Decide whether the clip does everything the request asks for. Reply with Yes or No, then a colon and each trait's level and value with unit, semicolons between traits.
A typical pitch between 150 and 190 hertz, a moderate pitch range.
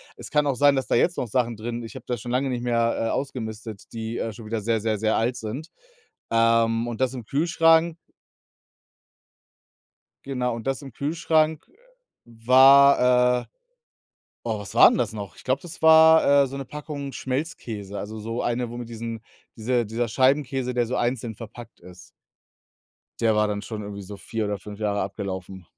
No: low, 120 Hz; average, 3.4 semitones